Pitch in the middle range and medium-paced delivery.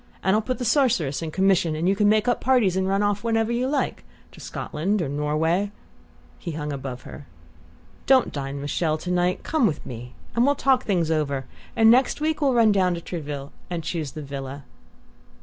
No: medium, 180 Hz; fast, 210 wpm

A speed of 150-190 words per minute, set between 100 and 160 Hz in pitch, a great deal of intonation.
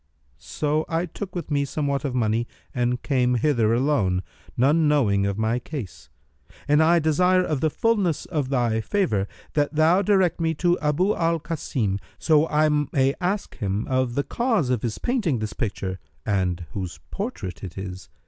Yes: average, 170 wpm; medium, 140 Hz; wide, 6.8 semitones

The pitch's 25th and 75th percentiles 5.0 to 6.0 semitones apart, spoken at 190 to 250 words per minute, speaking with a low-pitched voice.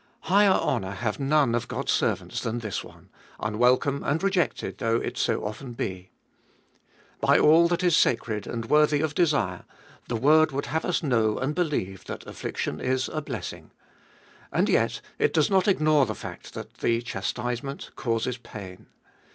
No: wide, 5.5 semitones; average, 165 wpm; low, 130 Hz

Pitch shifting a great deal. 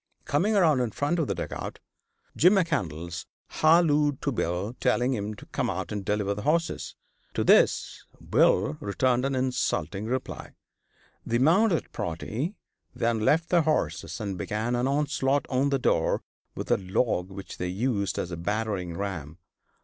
Yes: wide, 6.5 semitones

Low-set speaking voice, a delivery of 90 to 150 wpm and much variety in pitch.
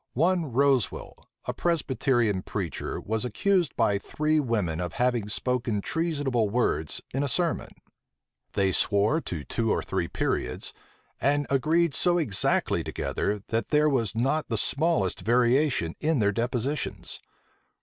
Yes: low, 125 Hz; slow, 135 wpm; wide, 6.3 semitones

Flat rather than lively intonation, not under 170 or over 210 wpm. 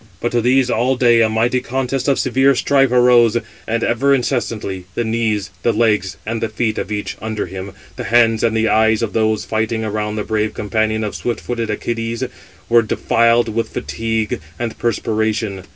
Yes: narrow, 1.7 semitones; average, 185 wpm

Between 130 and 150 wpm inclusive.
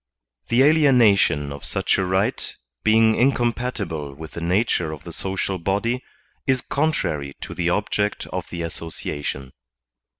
Yes: average, 145 wpm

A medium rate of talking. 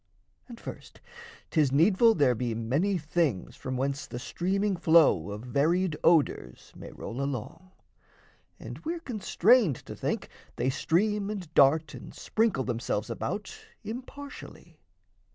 No: slow, 130 wpm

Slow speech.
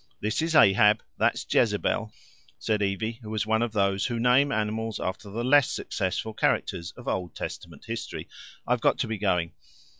No: average, 175 wpm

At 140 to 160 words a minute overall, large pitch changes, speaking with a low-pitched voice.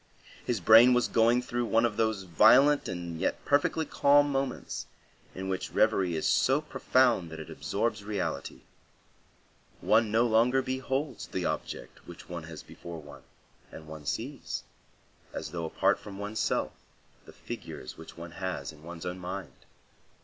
Yes: average, 155 wpm; wide, 6.1 semitones; low, 110 Hz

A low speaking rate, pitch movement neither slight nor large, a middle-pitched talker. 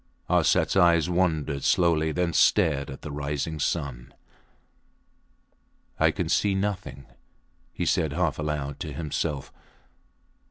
No: slow, 115 wpm; average, 3.3 semitones; very low, 80 Hz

